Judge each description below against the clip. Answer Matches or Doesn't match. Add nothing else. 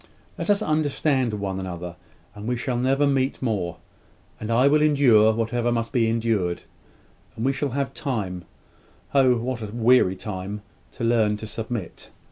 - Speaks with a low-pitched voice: Matches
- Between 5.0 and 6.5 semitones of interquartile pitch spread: Doesn't match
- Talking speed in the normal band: Matches